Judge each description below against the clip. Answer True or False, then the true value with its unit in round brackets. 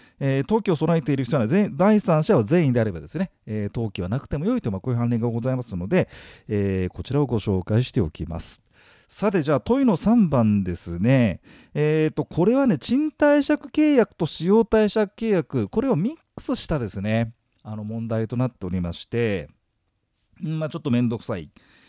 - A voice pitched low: True (130 Hz)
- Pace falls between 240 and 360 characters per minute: False (370 characters per minute)